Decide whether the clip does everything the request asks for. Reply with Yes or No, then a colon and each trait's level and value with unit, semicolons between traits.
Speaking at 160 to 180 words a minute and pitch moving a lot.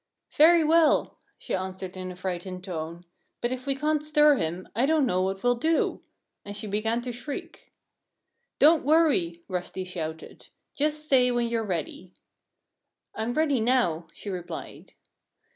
No: average, 150 wpm; wide, 7.8 semitones